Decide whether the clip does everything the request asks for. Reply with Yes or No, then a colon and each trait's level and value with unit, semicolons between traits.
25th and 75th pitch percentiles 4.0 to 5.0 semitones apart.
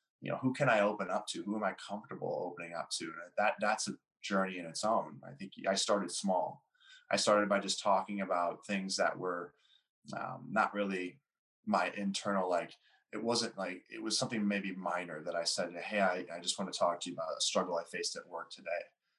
No: average, 3.5 semitones